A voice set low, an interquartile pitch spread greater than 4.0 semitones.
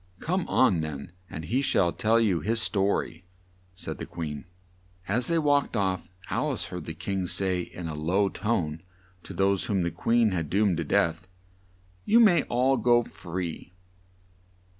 Yes: very low, 95 Hz; wide, 5.4 semitones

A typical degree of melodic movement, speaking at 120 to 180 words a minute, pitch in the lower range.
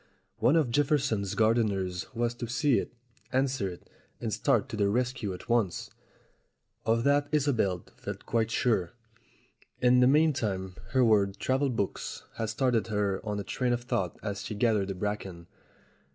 Yes: average, 4.1 semitones; average, 160 wpm; low, 115 Hz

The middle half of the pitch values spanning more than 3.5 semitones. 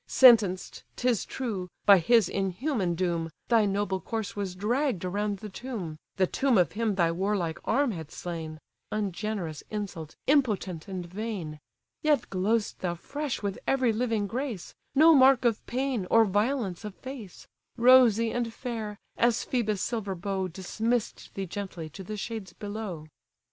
Yes: average, 4.4 semitones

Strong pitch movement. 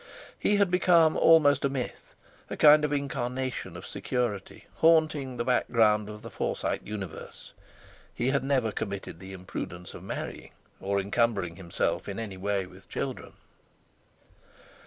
Yes: wide, 6.2 semitones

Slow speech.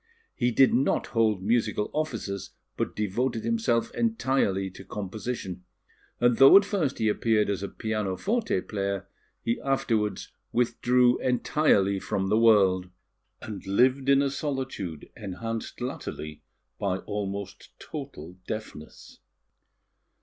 Yes: slow, 120 wpm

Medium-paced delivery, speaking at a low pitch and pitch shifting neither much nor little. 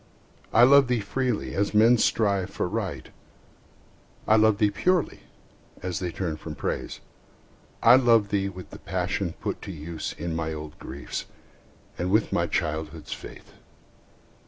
No: average, 150 wpm; low, 100 Hz; wide, 5.7 semitones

